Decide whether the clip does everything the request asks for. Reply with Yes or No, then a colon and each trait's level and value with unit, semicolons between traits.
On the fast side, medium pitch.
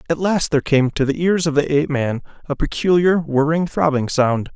Yes: fast, 210 wpm; medium, 150 Hz